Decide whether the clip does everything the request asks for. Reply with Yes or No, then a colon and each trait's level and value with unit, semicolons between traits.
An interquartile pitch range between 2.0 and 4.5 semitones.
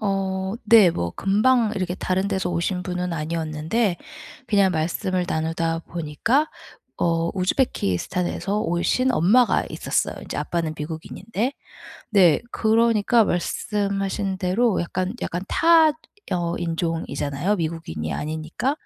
Yes: average, 4.1 semitones